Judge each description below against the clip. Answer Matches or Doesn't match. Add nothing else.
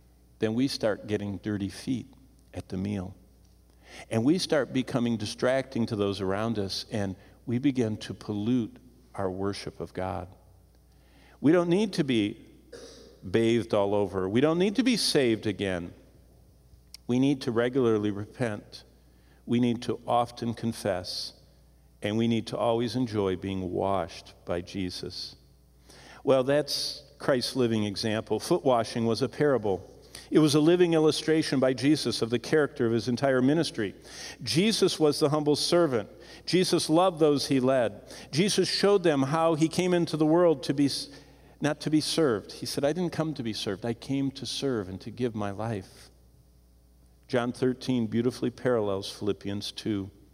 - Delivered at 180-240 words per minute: Doesn't match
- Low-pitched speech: Matches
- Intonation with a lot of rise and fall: Matches